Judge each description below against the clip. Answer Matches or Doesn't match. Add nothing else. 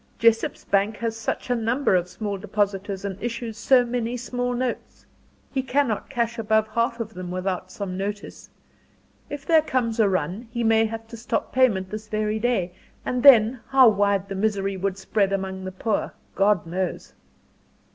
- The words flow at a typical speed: Matches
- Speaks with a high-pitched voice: Matches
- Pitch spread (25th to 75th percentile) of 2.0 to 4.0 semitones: Matches